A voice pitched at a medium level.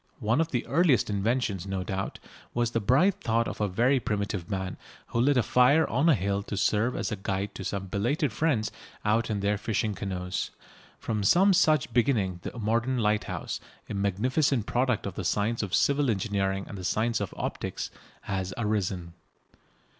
No: low, 110 Hz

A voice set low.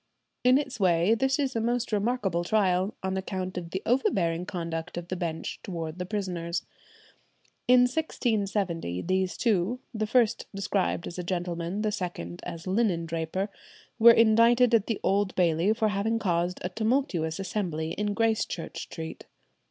No: high, 190 Hz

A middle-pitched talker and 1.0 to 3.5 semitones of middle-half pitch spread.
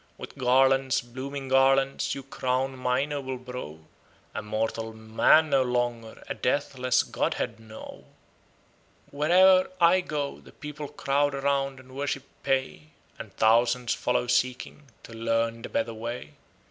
No: low, 130 Hz; average, 2.9 semitones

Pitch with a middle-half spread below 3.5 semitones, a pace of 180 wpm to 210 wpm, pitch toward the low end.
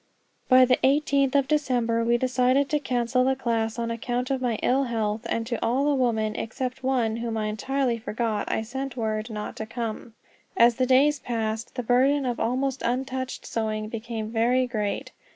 No: narrow, 2.5 semitones; average, 190 wpm; high, 240 Hz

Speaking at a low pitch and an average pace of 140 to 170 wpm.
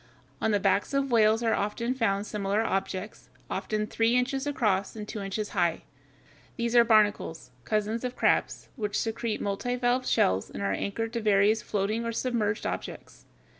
No: high, 215 Hz; average, 165 wpm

